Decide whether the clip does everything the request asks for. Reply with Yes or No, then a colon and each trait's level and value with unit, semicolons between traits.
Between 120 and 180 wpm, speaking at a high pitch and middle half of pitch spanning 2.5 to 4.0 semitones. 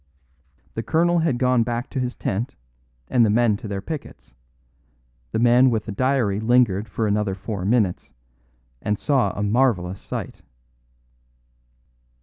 No: average, 140 wpm; low, 115 Hz; average, 3.6 semitones